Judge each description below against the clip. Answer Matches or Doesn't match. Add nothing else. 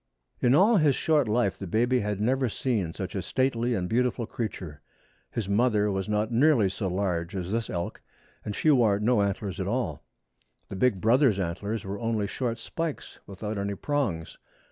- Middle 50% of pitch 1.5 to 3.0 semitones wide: Doesn't match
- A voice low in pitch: Matches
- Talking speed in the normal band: Matches